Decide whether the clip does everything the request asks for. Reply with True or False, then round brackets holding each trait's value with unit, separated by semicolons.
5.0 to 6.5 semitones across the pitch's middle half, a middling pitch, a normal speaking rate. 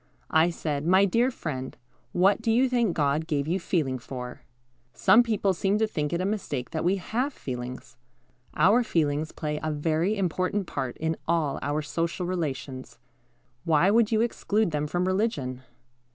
True (5.3 semitones; 170 Hz; 165 wpm)